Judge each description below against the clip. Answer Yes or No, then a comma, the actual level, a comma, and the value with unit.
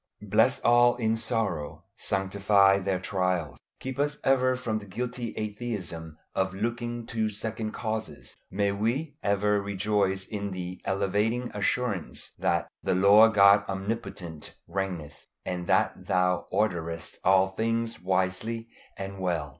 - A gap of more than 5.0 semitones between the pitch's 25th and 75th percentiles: No, average, 3.3 semitones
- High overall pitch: No, low, 100 Hz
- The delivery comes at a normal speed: No, slow, 130 wpm